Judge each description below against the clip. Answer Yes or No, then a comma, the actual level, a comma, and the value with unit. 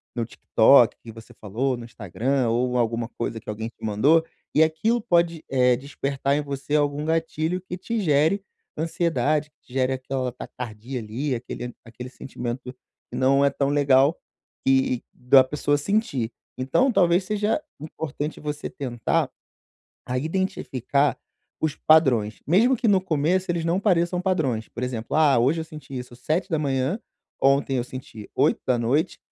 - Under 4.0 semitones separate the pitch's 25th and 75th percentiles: No, average, 4.5 semitones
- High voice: No, medium, 140 Hz